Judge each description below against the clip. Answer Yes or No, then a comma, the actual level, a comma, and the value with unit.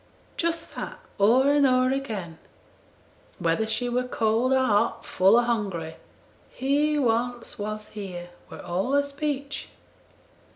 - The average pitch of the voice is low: No, high, 240 Hz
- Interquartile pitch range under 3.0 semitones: No, average, 4.9 semitones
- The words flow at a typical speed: No, slow, 130 wpm